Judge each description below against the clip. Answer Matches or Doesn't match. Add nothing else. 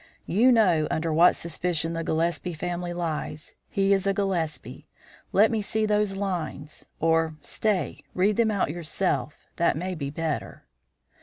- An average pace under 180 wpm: Matches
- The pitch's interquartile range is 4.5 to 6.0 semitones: Doesn't match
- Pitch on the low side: Doesn't match